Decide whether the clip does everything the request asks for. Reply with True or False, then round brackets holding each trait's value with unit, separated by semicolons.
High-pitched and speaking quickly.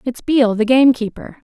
False (245 Hz; 155 wpm)